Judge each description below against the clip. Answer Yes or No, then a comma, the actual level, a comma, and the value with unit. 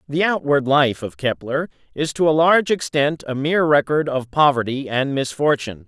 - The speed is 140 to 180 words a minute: Yes, average, 175 wpm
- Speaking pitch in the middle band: Yes, medium, 145 Hz